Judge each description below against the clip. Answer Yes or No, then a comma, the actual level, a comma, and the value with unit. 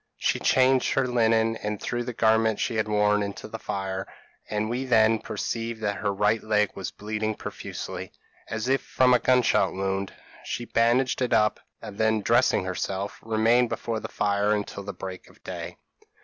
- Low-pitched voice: Yes, low, 110 Hz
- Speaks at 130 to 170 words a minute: No, average, 180 wpm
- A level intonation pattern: Yes, narrow, 2.2 semitones